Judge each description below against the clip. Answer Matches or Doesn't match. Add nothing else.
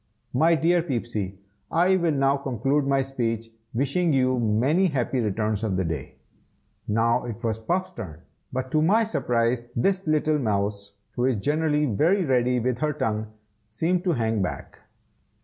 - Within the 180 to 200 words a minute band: Doesn't match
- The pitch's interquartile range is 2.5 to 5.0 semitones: Doesn't match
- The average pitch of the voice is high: Doesn't match